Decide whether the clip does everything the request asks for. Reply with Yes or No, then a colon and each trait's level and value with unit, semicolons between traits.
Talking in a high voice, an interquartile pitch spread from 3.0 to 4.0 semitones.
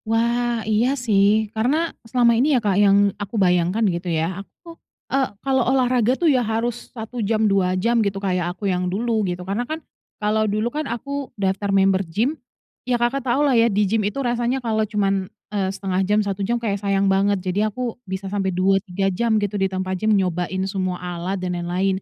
Yes: high, 205 Hz; average, 3.7 semitones